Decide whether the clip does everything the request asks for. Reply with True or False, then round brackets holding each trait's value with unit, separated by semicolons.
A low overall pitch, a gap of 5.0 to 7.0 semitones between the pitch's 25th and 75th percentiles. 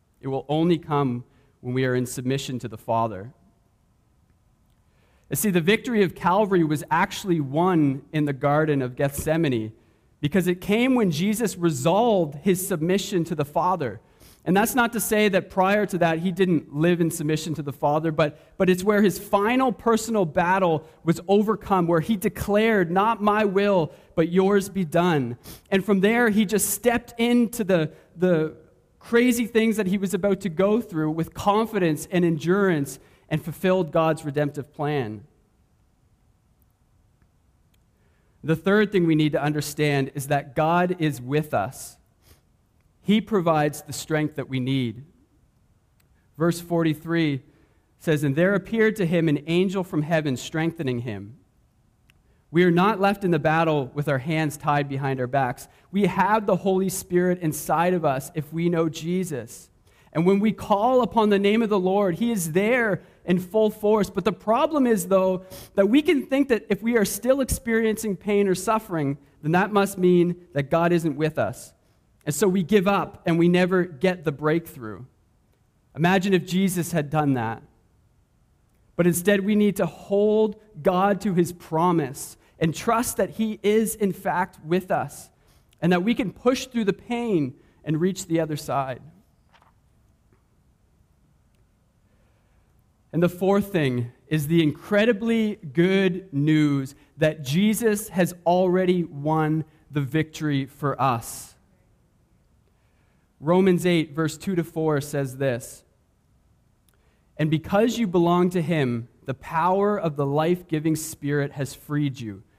False (170 Hz; 5.3 semitones)